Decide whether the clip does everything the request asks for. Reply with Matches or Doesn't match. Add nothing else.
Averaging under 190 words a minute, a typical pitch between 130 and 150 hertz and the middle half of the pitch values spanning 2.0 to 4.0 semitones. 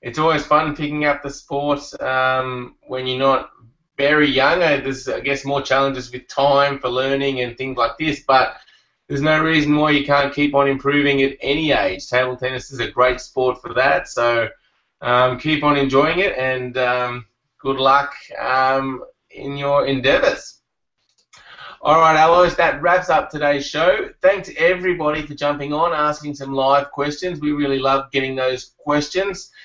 Matches